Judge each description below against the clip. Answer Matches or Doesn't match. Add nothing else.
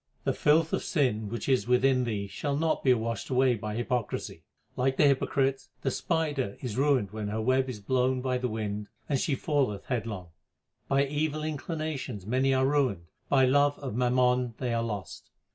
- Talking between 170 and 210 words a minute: Matches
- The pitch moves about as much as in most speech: Matches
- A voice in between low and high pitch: Doesn't match